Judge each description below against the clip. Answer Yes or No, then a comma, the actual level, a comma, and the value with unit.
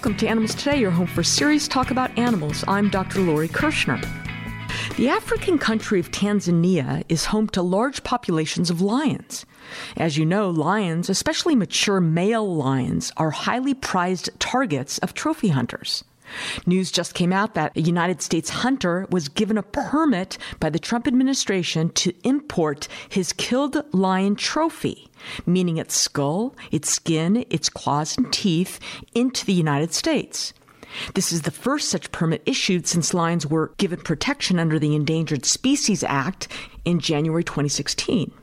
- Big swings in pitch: Yes, wide, 5.9 semitones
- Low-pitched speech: No, medium, 185 Hz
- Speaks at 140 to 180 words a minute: Yes, average, 155 wpm